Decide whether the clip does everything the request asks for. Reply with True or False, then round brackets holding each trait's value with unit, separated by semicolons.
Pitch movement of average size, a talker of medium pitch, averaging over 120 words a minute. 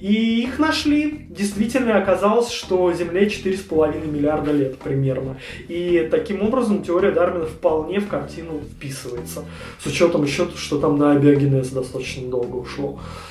False (6.5 semitones; 170 Hz; 135 wpm)